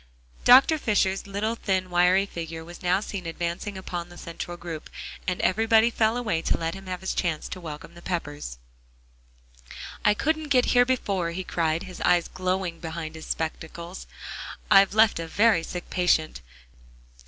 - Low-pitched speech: No, medium, 180 Hz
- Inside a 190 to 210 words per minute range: No, average, 165 wpm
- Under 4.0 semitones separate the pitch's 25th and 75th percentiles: Yes, average, 3.5 semitones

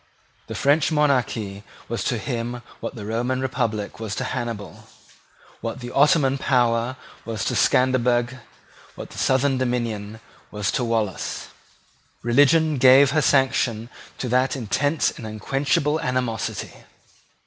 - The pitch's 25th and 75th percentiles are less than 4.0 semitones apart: Yes, average, 2.7 semitones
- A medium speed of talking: No, slow, 125 wpm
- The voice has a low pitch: Yes, low, 125 Hz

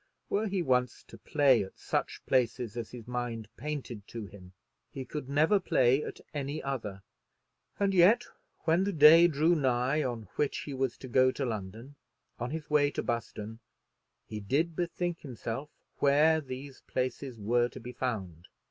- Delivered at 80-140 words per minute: No, average, 165 wpm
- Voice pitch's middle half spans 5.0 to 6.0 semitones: No, average, 4.3 semitones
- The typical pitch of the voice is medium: No, low, 130 Hz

